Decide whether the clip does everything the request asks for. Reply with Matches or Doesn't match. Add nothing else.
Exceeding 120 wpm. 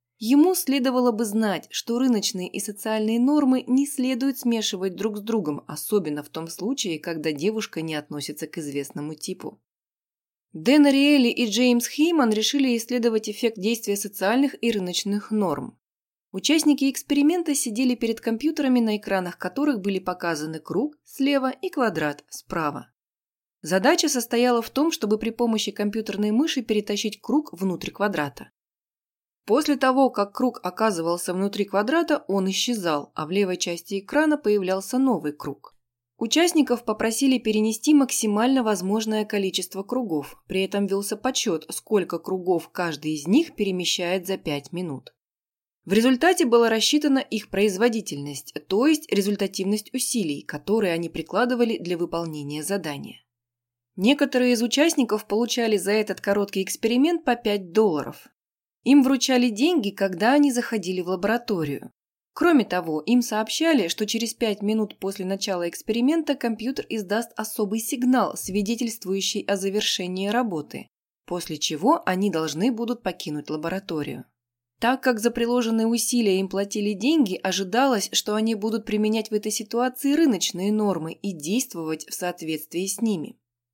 Matches